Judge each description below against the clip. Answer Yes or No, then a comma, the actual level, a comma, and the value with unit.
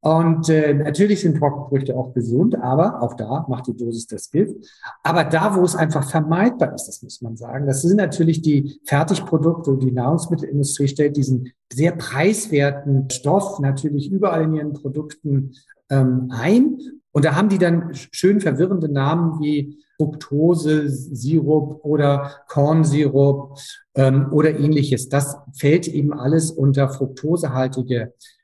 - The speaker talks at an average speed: Yes, average, 145 wpm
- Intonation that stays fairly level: No, average, 3.0 semitones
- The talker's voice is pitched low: No, medium, 150 Hz